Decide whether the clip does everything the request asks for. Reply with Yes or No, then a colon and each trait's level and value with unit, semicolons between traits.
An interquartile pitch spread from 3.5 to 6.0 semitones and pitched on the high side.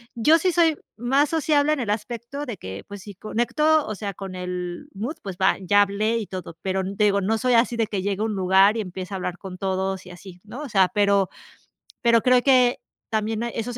Yes: average, 4.2 semitones; high, 210 Hz